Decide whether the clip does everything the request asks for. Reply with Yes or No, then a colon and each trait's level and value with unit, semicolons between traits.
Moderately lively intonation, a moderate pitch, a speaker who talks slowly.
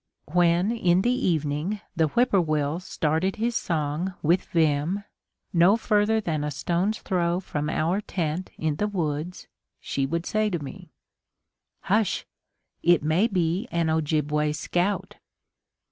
Yes: average, 4.0 semitones; medium, 170 Hz; slow, 130 wpm